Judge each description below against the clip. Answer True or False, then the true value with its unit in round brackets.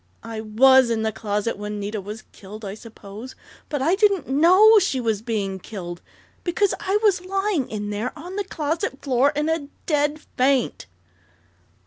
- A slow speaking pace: False (165 wpm)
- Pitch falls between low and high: False (260 Hz)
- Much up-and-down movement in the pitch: True (7.4 semitones)